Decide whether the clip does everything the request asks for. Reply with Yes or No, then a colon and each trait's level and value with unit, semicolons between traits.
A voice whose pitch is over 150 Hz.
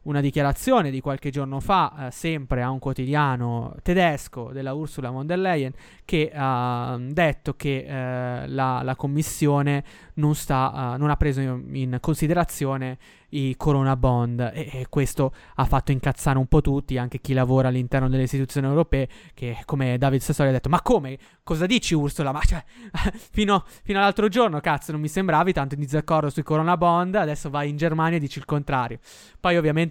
No: medium, 140 Hz